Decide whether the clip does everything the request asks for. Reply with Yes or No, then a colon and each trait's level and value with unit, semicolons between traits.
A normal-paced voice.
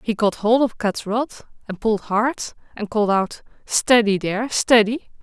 Yes: average, 170 wpm